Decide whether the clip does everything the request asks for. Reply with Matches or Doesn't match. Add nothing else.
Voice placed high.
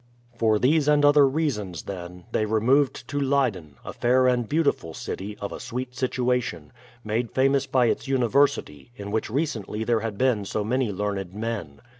Doesn't match